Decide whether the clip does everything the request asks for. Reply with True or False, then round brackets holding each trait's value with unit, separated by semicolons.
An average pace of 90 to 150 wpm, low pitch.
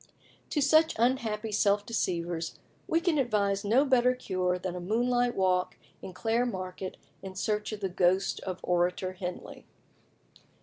False (145 wpm; 200 Hz)